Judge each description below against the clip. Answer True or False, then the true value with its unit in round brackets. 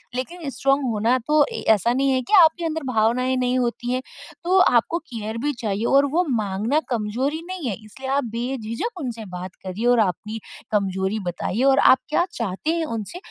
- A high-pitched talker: True (245 Hz)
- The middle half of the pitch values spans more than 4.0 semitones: True (4.6 semitones)